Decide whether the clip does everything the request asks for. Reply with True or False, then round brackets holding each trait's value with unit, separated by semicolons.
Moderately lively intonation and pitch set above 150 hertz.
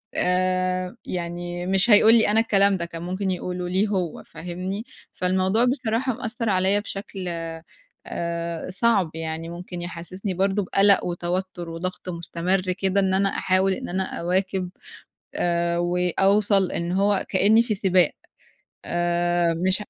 False (2.1 semitones; 185 Hz)